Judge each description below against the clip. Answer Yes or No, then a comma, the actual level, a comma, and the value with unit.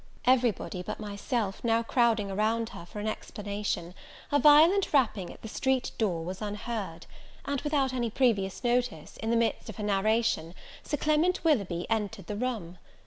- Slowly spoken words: No, average, 165 wpm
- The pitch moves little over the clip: No, average, 4.0 semitones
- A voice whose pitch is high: Yes, high, 220 Hz